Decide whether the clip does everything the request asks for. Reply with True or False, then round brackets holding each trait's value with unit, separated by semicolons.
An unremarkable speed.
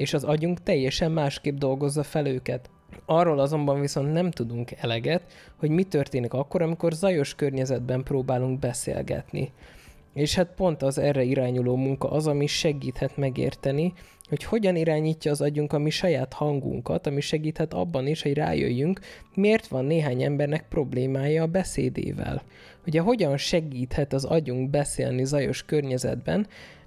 True (145 wpm)